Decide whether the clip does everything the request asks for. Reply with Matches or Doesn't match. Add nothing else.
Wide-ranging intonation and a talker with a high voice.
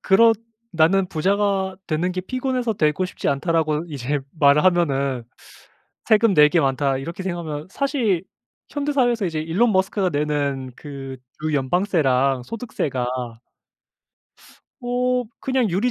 Doesn't match